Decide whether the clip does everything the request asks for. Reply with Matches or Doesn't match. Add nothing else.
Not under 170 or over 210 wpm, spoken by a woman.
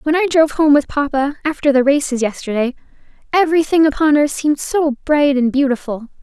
Matches